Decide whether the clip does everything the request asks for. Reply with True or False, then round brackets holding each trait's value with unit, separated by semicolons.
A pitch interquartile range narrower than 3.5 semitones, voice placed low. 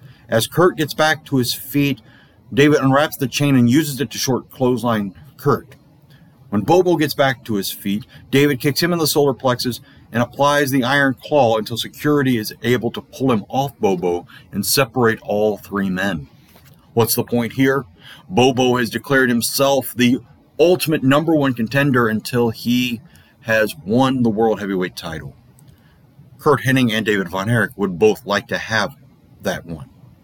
False (4.0 semitones; 125 Hz)